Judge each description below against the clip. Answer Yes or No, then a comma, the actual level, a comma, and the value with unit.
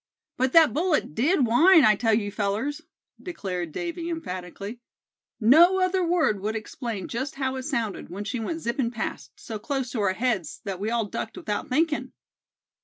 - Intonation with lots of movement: Yes, wide, 7.0 semitones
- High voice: Yes, high, 235 Hz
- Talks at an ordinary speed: Yes, average, 175 wpm